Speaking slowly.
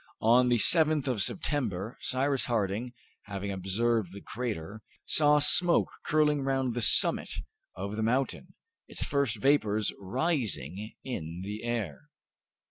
Yes: slow, 125 wpm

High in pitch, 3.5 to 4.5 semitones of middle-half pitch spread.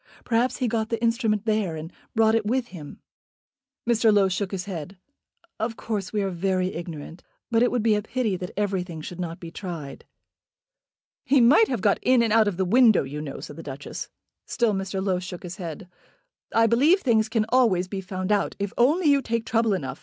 Yes: high, 205 Hz; average, 4.0 semitones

